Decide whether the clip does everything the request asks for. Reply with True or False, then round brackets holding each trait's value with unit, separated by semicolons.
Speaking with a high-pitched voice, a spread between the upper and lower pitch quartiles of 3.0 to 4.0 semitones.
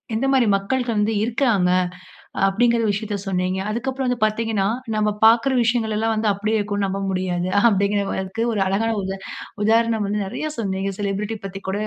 False (210 Hz; 2.6 semitones)